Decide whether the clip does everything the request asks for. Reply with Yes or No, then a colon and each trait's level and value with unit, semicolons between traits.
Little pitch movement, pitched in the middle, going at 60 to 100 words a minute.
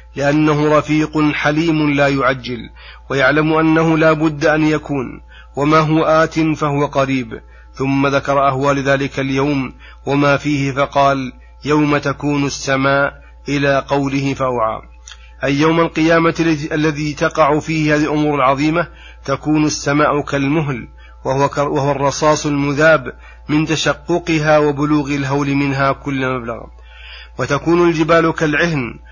No: narrow, 2.0 semitones; medium, 145 Hz; average, 115 wpm